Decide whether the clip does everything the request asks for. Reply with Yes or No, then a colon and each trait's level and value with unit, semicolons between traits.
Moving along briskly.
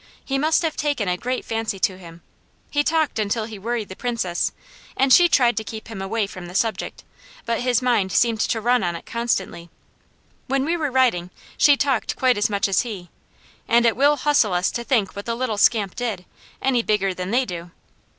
Yes: fast, 210 wpm